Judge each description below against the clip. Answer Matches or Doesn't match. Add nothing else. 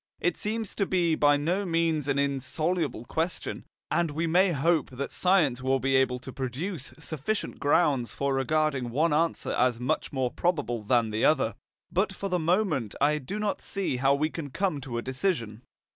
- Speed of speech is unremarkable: Matches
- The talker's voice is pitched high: Doesn't match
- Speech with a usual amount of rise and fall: Matches